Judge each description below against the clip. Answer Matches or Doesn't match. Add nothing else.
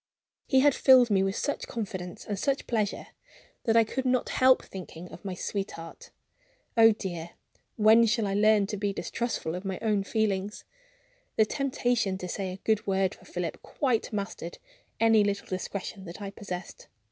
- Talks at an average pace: Matches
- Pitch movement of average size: Matches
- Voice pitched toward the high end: Matches